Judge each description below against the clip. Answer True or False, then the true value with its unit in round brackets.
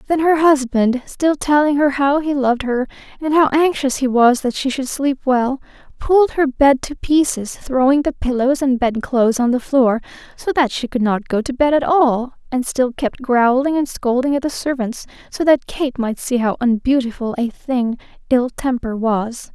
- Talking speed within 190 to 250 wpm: True (195 wpm)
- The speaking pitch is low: False (265 Hz)